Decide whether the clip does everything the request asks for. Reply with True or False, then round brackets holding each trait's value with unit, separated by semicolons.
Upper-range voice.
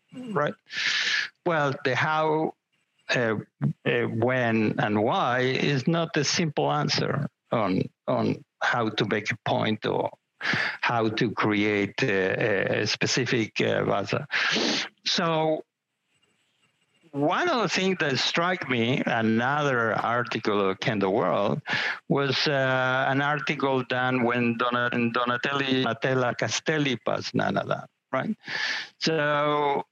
False (130 Hz)